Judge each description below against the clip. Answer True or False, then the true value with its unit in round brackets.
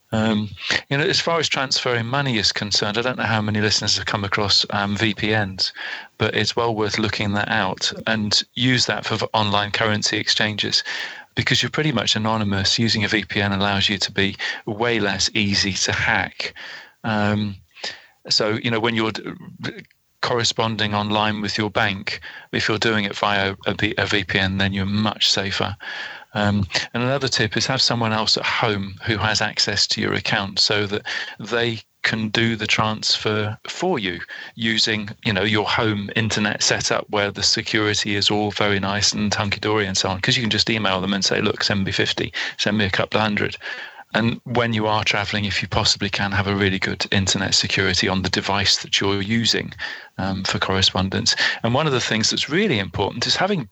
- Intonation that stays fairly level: True (1.9 semitones)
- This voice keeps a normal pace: True (190 wpm)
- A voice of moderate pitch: False (105 Hz)